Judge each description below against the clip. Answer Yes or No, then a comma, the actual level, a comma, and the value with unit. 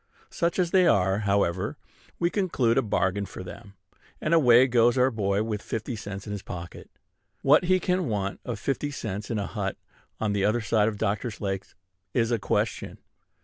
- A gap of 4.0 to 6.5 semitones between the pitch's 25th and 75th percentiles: Yes, average, 4.7 semitones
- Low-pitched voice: Yes, low, 110 Hz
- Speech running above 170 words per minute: Yes, average, 190 wpm